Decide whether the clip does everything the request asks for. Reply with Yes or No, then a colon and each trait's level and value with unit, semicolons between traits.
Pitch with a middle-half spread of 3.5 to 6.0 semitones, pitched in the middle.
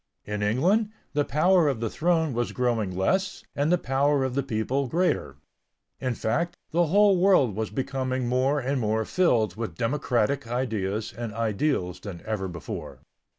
No: average, 5.3 semitones; low, 130 Hz